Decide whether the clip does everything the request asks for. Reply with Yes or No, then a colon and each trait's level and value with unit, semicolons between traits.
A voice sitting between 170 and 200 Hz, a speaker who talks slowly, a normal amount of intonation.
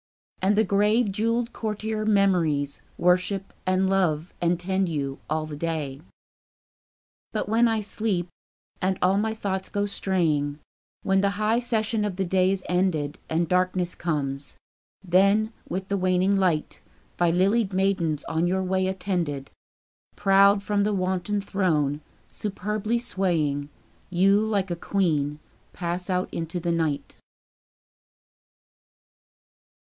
Yes: medium, 185 Hz; slow, 130 wpm; average, 3.1 semitones